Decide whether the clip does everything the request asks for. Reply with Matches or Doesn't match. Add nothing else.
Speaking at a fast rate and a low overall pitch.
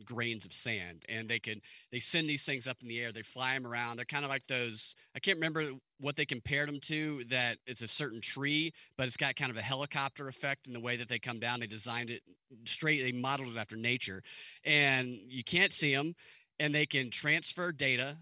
Matches